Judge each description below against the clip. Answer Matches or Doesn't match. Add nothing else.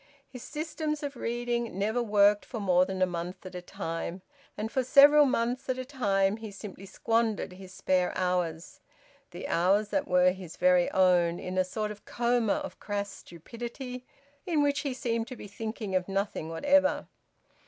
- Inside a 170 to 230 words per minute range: Matches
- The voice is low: Doesn't match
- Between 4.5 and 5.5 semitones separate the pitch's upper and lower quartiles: Matches